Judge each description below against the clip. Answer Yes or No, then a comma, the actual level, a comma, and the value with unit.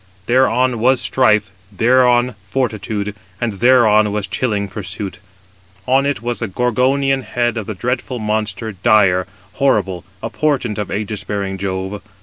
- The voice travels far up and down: No, average, 3.7 semitones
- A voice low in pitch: Yes, low, 110 Hz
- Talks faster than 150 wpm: No, average, 140 wpm